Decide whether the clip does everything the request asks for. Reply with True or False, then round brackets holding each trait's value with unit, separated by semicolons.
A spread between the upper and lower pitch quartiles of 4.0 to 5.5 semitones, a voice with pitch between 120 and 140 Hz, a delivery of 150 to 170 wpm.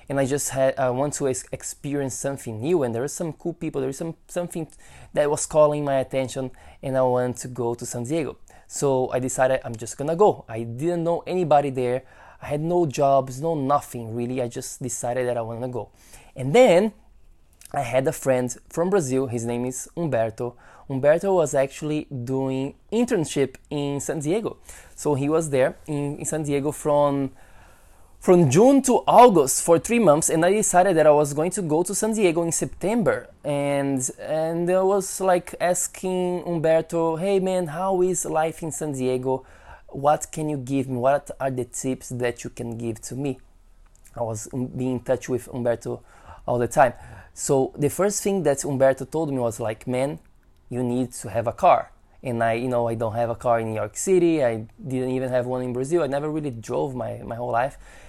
False (4.5 semitones; 135 Hz; 200 wpm)